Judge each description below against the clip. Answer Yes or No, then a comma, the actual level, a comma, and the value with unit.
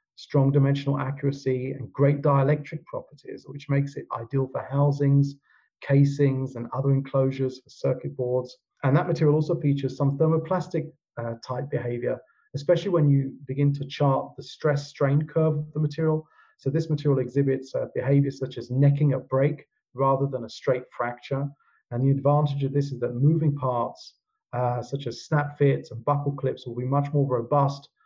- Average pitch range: No, narrow, 1.7 semitones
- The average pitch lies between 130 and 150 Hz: Yes, medium, 140 Hz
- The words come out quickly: No, average, 175 wpm